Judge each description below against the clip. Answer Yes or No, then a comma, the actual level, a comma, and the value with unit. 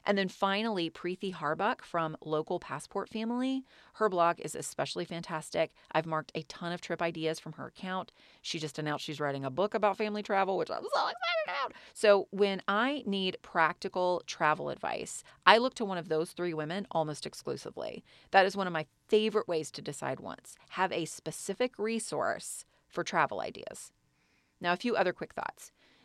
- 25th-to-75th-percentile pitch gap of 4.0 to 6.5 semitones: Yes, average, 4.3 semitones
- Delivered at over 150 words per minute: Yes, average, 180 wpm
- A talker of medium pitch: Yes, medium, 180 Hz